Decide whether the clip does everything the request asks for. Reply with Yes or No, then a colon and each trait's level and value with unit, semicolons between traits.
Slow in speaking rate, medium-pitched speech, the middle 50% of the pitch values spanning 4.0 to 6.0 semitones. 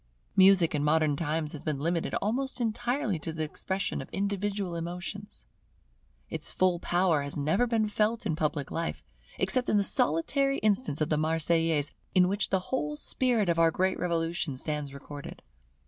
No: average, 165 wpm; medium, 175 Hz; average, 4.8 semitones